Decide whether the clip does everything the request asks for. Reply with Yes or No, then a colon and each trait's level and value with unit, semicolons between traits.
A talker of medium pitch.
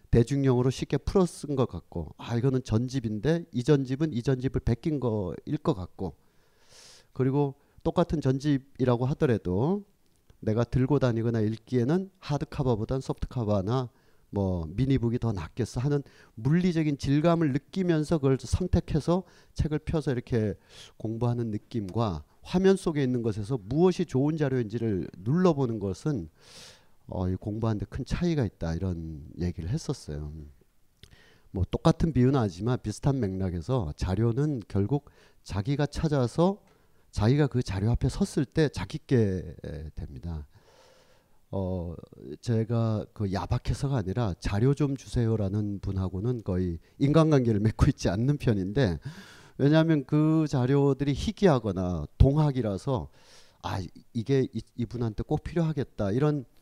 No: low, 125 Hz